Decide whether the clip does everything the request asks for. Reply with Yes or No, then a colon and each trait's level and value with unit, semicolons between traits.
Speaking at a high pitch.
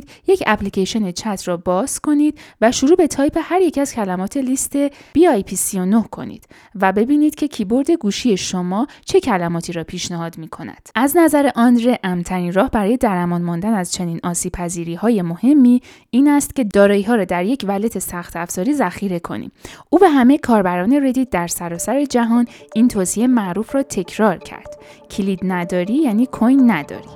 Yes: high, 215 Hz